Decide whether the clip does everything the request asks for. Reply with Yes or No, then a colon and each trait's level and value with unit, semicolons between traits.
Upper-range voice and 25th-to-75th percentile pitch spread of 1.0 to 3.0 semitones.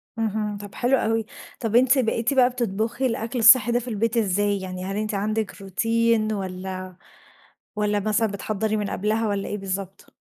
Yes: high, 215 Hz; narrow, 2.5 semitones